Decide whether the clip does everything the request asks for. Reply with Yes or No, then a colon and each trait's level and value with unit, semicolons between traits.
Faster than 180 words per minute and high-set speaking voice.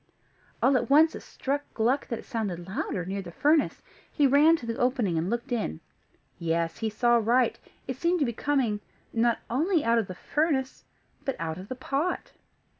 Yes: average, 190 wpm; high, 240 Hz